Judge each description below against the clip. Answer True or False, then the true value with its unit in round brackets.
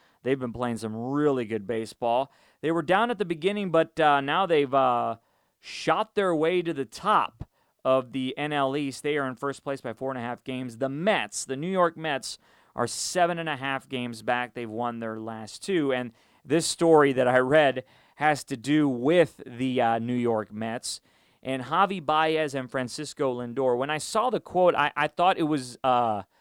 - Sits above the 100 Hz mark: True (135 Hz)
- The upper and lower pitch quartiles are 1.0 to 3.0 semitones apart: False (4.2 semitones)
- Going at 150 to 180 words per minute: False (200 wpm)